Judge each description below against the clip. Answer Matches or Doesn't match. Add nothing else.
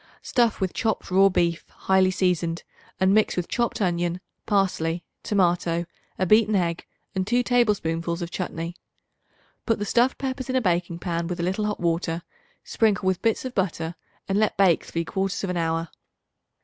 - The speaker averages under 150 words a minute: Doesn't match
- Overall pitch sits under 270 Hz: Matches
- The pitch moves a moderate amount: Matches